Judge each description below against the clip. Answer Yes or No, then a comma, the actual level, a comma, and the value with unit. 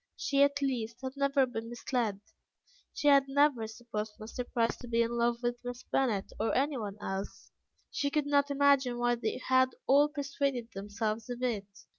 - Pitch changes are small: No, average, 3.5 semitones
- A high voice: Yes, high, 245 Hz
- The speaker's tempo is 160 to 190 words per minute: Yes, average, 175 wpm